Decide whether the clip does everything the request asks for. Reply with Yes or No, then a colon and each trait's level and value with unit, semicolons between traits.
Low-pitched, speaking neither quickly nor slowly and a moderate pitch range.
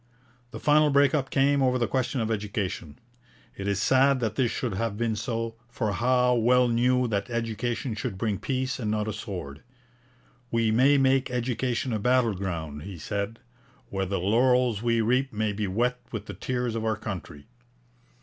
Yes: low, 115 Hz; average, 180 wpm; average, 3.6 semitones